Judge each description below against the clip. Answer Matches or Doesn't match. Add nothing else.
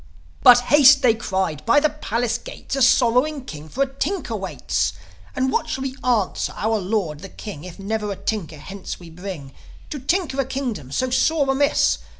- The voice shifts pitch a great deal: Matches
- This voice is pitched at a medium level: Doesn't match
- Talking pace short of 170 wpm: Doesn't match